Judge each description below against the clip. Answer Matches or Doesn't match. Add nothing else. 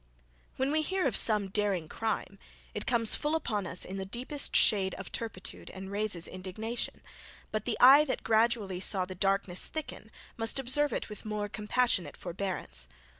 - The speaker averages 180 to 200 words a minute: Doesn't match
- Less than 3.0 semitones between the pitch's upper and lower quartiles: Doesn't match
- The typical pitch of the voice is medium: Doesn't match